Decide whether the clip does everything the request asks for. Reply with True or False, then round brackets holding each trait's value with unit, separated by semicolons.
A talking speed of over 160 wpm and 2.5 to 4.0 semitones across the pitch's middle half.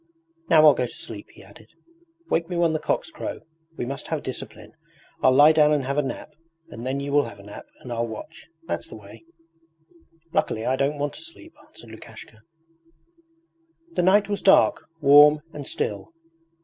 False (190 wpm; 5.1 semitones)